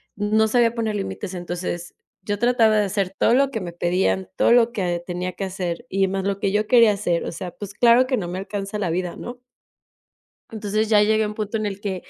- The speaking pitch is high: Yes, high, 205 Hz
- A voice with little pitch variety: No, average, 3.1 semitones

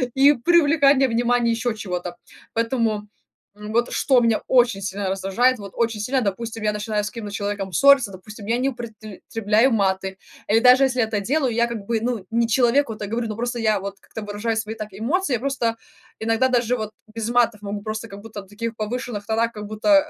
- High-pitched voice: Yes, high, 225 Hz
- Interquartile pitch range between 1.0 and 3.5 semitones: Yes, average, 2.7 semitones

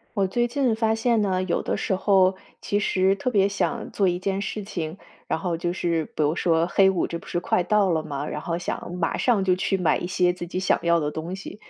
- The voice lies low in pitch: No, medium, 185 Hz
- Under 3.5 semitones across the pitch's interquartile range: Yes, average, 2.8 semitones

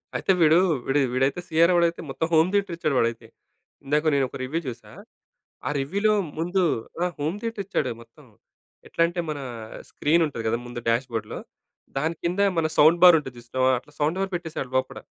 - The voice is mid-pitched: Yes, medium, 155 Hz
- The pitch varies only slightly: No, average, 4.7 semitones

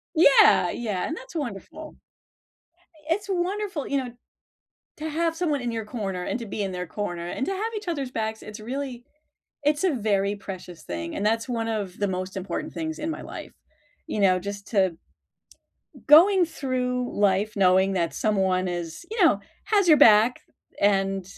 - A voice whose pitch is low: No, high, 220 Hz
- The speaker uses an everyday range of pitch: No, wide, 7.8 semitones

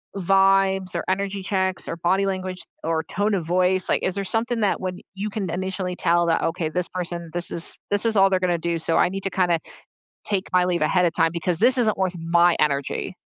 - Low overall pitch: No, medium, 185 Hz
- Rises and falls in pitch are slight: Yes, narrow, 2.1 semitones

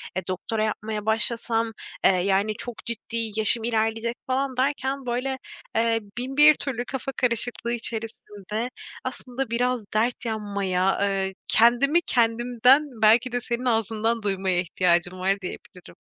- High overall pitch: Yes, high, 230 Hz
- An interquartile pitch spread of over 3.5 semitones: No, average, 2.9 semitones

